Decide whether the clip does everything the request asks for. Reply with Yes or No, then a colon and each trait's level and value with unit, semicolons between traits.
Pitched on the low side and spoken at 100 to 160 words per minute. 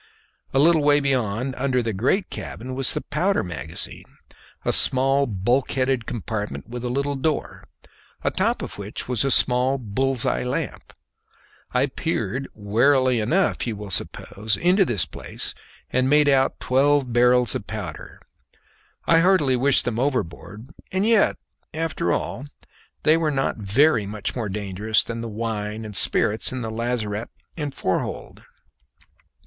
Yes: low, 125 Hz; average, 150 wpm